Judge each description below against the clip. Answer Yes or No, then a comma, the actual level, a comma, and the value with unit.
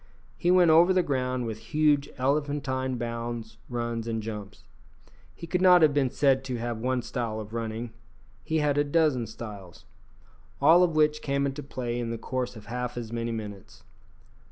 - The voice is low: Yes, low, 125 Hz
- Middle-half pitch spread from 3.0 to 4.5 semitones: Yes, average, 4.1 semitones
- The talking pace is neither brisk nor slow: Yes, average, 180 wpm